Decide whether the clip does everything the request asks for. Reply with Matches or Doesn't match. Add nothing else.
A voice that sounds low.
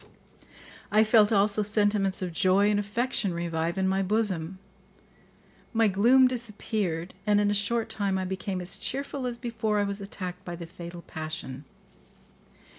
Doesn't match